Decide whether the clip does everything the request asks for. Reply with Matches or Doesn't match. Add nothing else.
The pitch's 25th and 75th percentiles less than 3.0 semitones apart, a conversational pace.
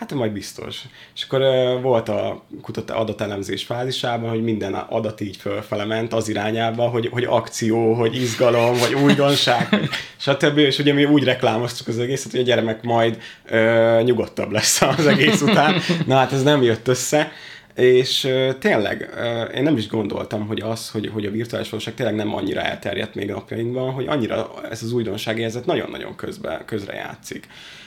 Doesn't match